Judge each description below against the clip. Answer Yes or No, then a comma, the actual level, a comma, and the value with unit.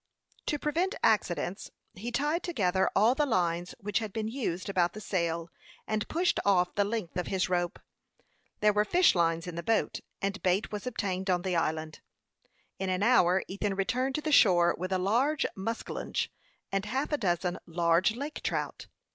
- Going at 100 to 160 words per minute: No, average, 180 wpm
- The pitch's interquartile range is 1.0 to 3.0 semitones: No, average, 4.6 semitones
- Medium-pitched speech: No, high, 195 Hz